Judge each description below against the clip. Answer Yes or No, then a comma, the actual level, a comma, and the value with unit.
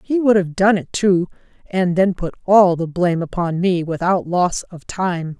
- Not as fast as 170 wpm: No, average, 200 wpm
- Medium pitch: Yes, medium, 180 Hz